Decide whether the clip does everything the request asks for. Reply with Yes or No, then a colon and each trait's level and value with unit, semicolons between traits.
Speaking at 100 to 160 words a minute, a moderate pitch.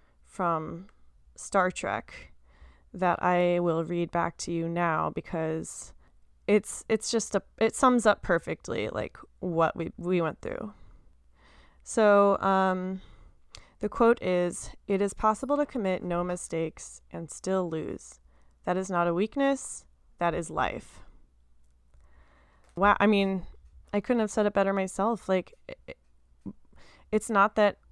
Yes: average, 140 wpm; medium, 175 Hz